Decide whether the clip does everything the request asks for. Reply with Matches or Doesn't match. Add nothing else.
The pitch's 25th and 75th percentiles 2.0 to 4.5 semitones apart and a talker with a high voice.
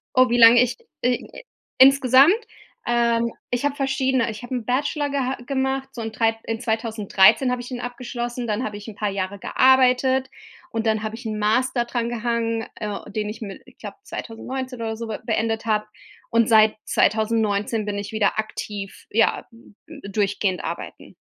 Matches